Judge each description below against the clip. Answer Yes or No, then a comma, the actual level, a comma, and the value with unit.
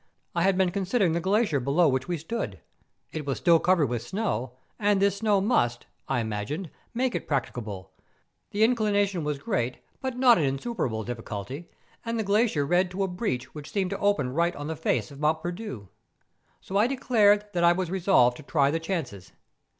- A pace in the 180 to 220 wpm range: Yes, average, 190 wpm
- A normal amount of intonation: No, wide, 6.8 semitones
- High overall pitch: No, medium, 170 Hz